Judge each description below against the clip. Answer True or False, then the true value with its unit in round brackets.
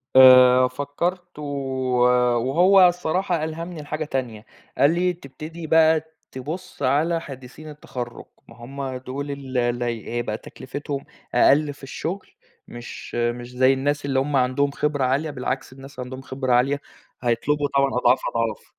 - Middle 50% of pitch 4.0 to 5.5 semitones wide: False (3.5 semitones)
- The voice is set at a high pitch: False (140 Hz)